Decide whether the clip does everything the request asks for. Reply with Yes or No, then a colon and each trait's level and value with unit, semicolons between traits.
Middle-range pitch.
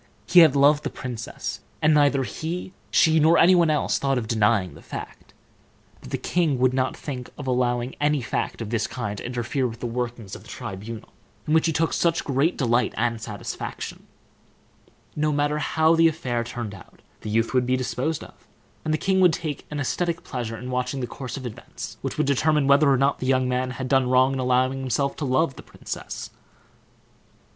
No: low, 130 Hz